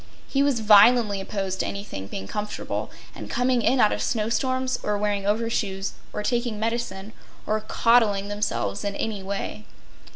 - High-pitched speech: Yes, high, 210 Hz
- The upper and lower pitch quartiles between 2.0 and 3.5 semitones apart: Yes, average, 2.8 semitones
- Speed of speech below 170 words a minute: Yes, average, 160 wpm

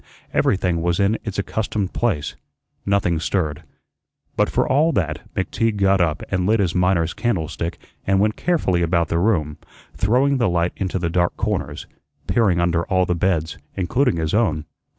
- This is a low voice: Yes, very low, 90 Hz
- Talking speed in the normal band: Yes, average, 165 wpm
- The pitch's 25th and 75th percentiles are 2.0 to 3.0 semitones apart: No, average, 3.8 semitones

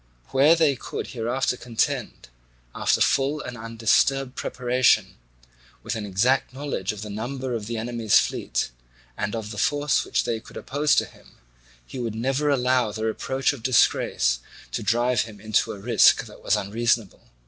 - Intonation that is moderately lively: Yes, average, 3.4 semitones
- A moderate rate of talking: Yes, average, 165 wpm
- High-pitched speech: No, low, 120 Hz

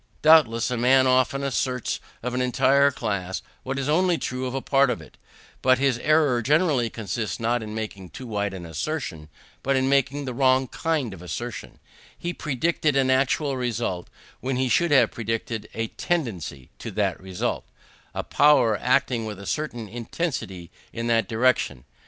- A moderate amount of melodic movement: Yes, average, 3.8 semitones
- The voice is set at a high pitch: No, low, 125 Hz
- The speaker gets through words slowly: No, average, 175 wpm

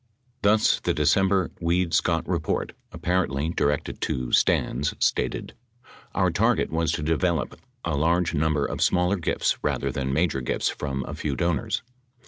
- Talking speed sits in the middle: Yes, average, 150 wpm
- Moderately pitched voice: No, very low, 80 Hz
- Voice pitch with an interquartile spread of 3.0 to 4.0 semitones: Yes, average, 3.7 semitones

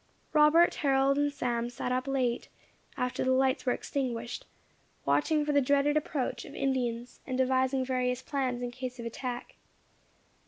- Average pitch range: No, narrow, 2.0 semitones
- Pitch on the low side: No, very high, 260 Hz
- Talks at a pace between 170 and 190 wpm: No, average, 155 wpm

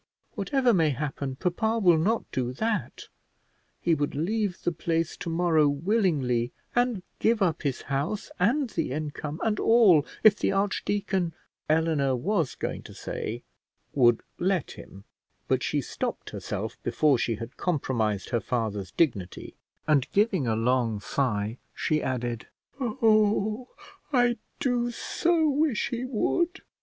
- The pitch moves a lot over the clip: Yes, wide, 8.7 semitones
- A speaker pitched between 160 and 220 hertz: Yes, medium, 165 Hz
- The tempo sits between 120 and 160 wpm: Yes, average, 140 wpm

